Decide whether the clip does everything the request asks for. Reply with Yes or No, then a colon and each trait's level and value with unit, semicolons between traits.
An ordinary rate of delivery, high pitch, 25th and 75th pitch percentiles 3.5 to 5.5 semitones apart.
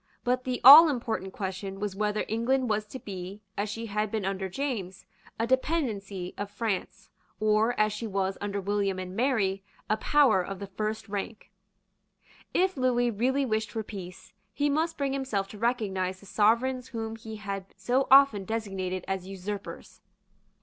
Yes: average, 165 wpm; high, 215 Hz; average, 4.0 semitones